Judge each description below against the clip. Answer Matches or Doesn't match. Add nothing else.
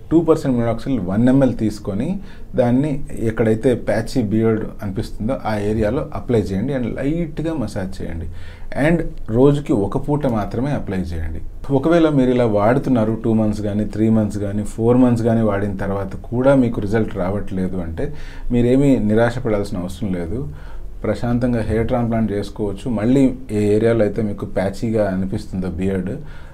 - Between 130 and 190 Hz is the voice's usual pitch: Doesn't match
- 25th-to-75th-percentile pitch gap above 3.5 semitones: Matches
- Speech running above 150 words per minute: Doesn't match